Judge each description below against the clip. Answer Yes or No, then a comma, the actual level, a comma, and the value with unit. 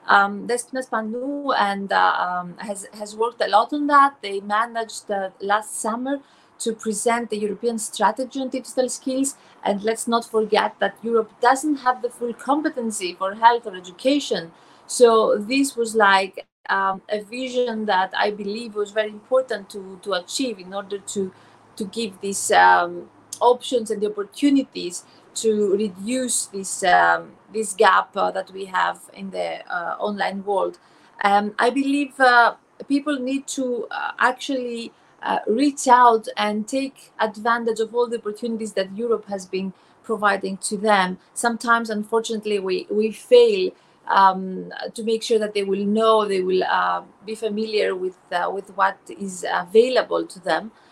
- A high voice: Yes, high, 220 Hz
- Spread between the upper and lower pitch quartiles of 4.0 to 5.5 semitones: No, average, 3.6 semitones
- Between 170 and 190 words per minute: No, average, 160 wpm